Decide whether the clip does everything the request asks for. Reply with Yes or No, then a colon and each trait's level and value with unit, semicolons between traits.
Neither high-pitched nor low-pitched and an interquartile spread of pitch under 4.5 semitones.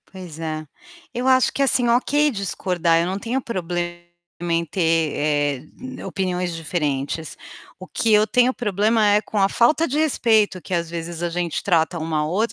No: medium, 180 Hz; average, 5.1 semitones